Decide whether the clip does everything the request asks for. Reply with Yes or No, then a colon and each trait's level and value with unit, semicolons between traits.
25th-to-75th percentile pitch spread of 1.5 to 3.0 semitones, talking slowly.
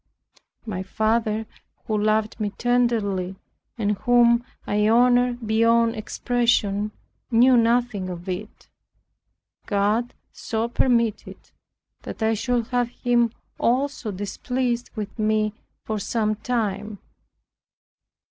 Yes: narrow, 2.4 semitones; slow, 105 wpm